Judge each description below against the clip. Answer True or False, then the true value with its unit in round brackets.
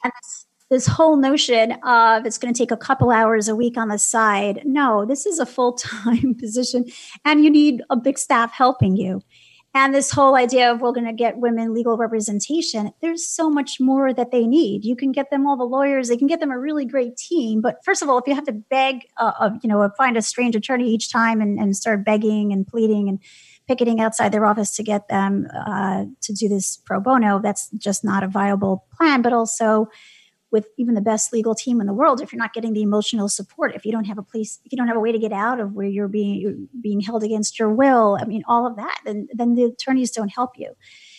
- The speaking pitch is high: True (230 Hz)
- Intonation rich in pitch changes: False (3.5 semitones)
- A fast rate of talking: True (235 wpm)